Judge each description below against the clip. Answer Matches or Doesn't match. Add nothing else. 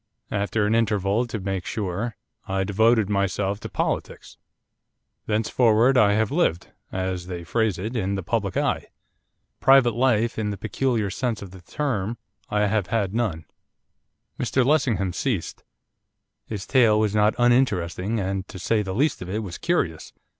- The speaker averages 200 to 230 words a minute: Doesn't match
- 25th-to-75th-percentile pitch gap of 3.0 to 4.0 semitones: Matches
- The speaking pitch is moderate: Doesn't match